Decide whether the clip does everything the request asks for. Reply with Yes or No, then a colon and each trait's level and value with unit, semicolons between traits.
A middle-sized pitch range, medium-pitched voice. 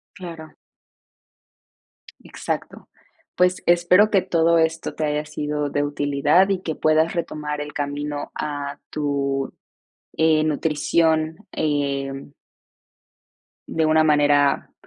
No: narrow, 2.0 semitones; medium, 150 Hz